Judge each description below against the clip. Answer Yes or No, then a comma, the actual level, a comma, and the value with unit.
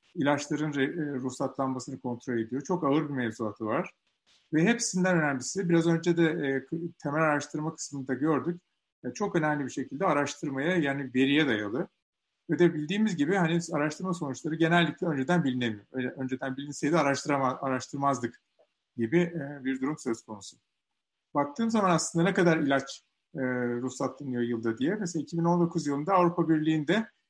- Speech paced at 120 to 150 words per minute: Yes, average, 130 wpm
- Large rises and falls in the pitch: No, average, 4.0 semitones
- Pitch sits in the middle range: Yes, medium, 145 Hz